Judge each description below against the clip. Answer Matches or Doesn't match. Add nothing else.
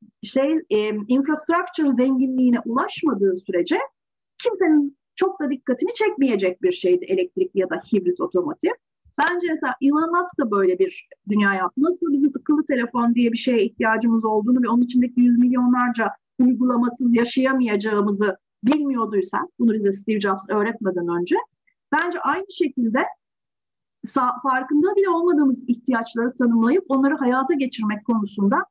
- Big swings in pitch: Matches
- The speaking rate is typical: Matches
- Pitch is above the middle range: Matches